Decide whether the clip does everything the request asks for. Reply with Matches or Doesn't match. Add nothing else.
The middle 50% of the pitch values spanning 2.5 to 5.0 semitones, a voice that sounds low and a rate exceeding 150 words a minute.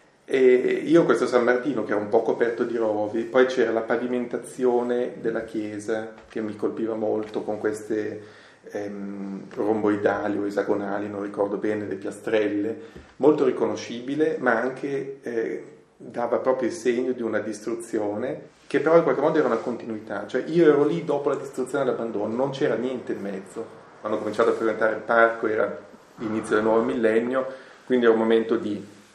Matches